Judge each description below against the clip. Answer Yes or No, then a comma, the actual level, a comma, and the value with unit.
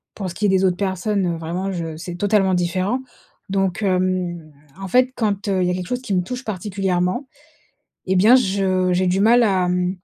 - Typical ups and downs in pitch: No, narrow, 2.2 semitones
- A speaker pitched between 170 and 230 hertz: Yes, high, 190 Hz